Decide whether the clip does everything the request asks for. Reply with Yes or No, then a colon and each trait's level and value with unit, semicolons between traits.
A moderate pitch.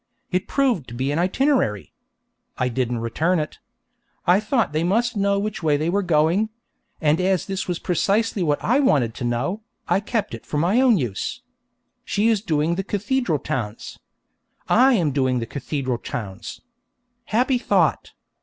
Yes: medium, 175 Hz